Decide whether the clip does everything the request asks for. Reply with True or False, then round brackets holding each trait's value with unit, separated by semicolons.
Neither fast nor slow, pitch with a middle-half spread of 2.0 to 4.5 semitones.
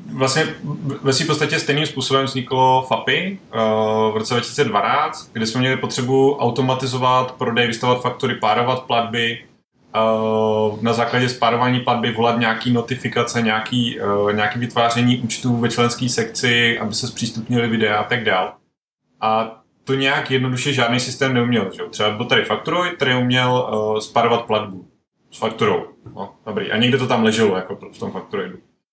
True (145 wpm; 2.4 semitones)